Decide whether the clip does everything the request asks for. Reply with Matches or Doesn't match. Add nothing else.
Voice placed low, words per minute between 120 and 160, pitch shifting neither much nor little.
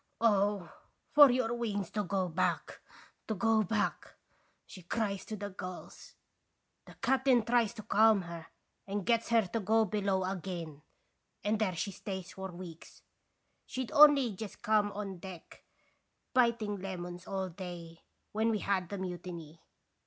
Doesn't match